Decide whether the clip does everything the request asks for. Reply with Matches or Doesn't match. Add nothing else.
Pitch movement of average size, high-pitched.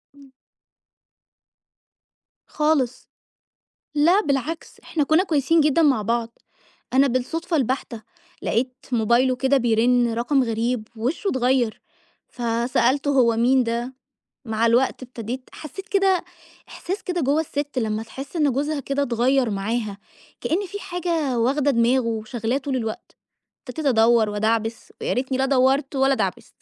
Matches